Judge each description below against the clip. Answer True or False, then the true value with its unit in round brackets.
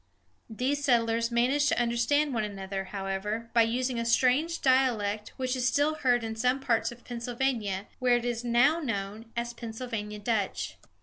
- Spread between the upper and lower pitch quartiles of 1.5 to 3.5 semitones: True (2.6 semitones)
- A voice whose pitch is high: True (235 Hz)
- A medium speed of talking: True (165 wpm)